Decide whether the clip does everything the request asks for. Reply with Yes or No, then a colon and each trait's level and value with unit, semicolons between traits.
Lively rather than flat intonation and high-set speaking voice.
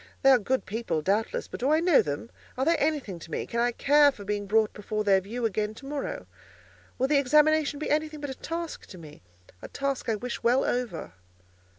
Yes: wide, 6.0 semitones; high, 245 Hz